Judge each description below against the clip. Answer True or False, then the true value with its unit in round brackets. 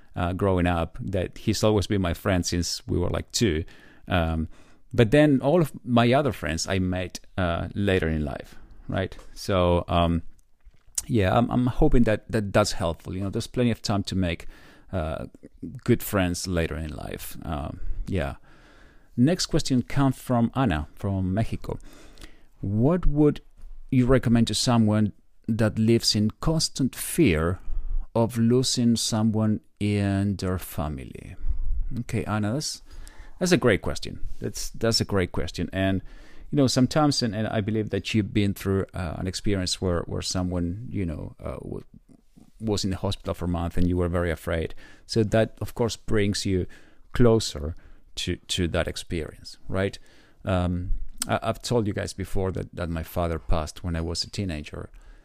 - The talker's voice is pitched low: True (100 Hz)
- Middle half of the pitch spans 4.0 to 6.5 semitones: True (4.6 semitones)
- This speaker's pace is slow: False (165 wpm)